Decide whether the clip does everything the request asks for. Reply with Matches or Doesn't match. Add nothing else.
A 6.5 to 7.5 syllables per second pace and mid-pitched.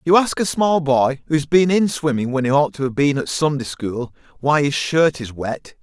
Doesn't match